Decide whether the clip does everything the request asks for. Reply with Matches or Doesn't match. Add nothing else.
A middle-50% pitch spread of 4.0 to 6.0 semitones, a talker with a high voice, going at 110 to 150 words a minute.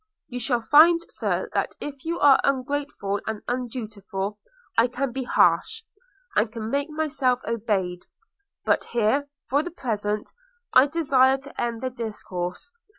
Matches